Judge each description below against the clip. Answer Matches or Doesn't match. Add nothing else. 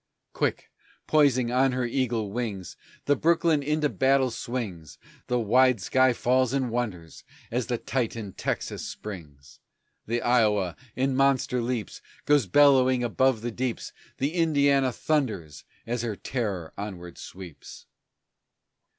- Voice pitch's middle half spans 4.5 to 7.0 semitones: Doesn't match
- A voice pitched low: Matches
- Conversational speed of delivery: Doesn't match